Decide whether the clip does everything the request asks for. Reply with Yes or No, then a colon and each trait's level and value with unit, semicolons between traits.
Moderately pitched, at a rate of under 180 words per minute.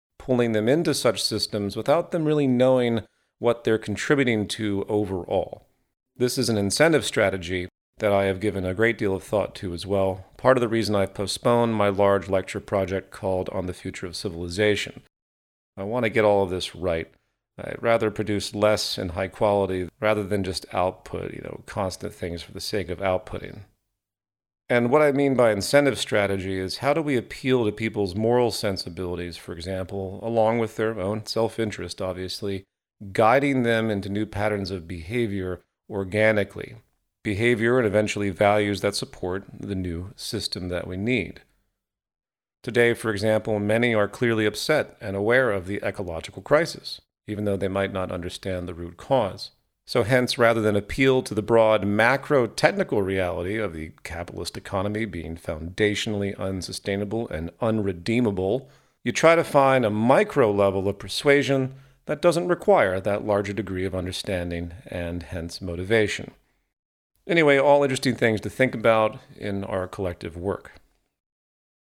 No: low, 105 Hz; average, 160 wpm